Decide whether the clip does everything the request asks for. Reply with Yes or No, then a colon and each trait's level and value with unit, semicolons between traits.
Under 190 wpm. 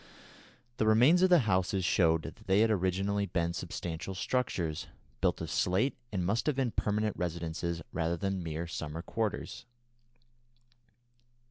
Yes: average, 140 wpm